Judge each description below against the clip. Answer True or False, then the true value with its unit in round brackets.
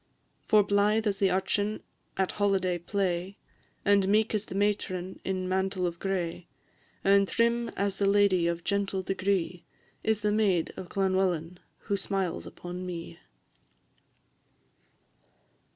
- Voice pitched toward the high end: True (195 Hz)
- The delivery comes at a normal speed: False (130 wpm)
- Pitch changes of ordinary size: False (1.9 semitones)